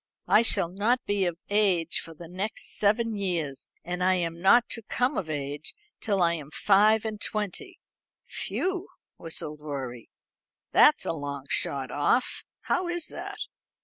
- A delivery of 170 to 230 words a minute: No, average, 150 wpm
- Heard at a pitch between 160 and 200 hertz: Yes, medium, 185 Hz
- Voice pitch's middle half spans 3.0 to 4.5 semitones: No, wide, 5.6 semitones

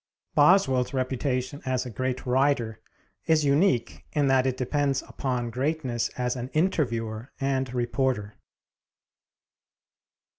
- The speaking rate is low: Yes, slow, 110 wpm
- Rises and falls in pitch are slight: Yes, narrow, 2.3 semitones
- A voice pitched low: Yes, low, 130 Hz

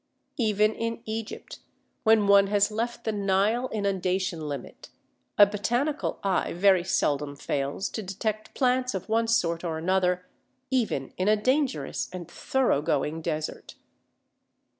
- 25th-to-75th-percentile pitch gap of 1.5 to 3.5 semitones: No, average, 4.2 semitones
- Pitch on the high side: Yes, high, 200 Hz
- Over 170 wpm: No, slow, 135 wpm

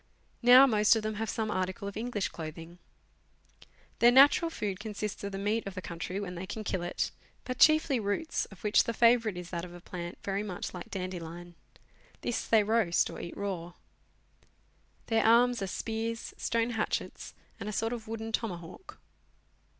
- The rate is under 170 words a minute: No, average, 180 wpm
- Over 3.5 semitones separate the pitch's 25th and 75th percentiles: Yes, average, 3.9 semitones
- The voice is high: Yes, high, 210 Hz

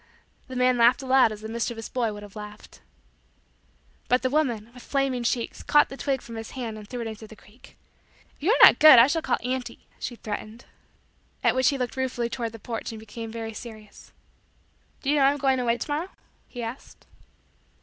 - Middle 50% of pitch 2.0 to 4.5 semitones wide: Yes, average, 2.8 semitones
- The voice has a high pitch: Yes, high, 240 Hz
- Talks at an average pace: No, fast, 215 wpm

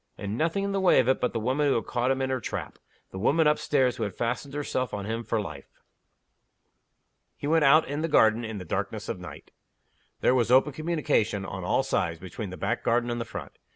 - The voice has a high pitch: No, low, 125 Hz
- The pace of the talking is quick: Yes, fast, 240 wpm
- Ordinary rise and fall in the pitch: Yes, average, 4.9 semitones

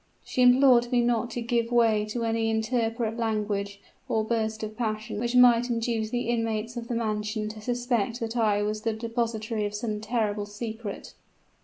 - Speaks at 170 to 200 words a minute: Yes, average, 175 wpm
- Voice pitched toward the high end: Yes, high, 225 Hz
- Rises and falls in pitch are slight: Yes, narrow, 1.7 semitones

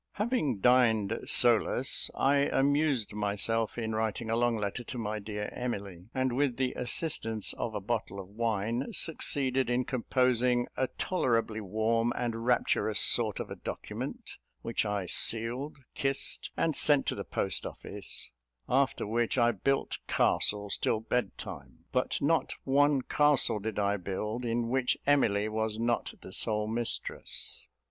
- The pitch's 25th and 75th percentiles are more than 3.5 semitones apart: No, average, 3.2 semitones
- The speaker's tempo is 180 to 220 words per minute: No, average, 150 wpm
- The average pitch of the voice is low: Yes, low, 115 Hz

